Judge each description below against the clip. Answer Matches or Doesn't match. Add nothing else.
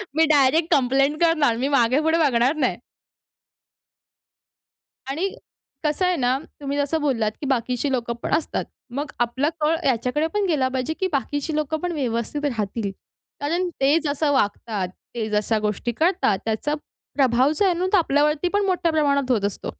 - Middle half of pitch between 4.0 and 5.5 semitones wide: Matches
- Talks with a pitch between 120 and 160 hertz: Doesn't match